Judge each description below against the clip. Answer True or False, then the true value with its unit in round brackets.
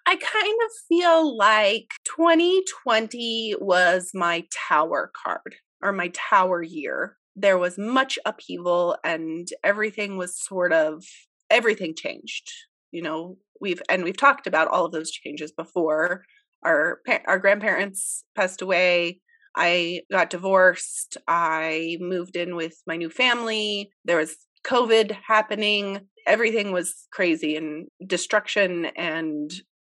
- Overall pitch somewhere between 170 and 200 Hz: True (190 Hz)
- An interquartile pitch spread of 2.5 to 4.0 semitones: False (4.6 semitones)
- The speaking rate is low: True (125 wpm)